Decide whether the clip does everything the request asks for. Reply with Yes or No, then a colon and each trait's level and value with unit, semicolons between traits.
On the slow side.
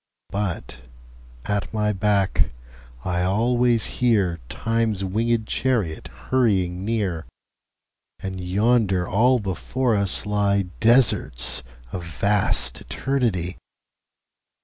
Yes: slow, 80 wpm